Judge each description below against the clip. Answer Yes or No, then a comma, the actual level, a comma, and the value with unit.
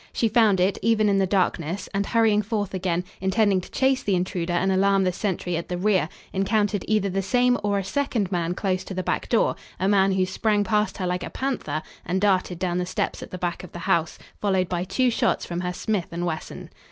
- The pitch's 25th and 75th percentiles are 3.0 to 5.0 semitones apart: No, narrow, 2.6 semitones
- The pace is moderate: No, fast, 230 wpm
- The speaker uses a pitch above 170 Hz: Yes, high, 190 Hz